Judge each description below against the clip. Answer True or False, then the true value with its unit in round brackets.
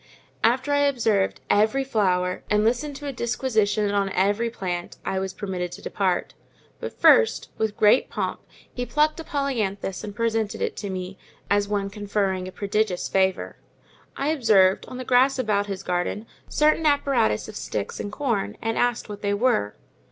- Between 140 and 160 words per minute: False (175 wpm)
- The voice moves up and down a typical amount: True (4.4 semitones)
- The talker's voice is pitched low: False (210 Hz)